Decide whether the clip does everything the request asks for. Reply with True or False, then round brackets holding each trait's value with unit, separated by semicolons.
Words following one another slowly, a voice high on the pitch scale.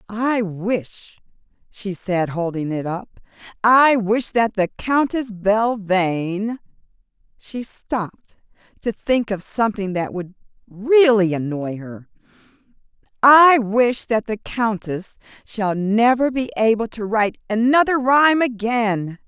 True (115 wpm; 215 Hz)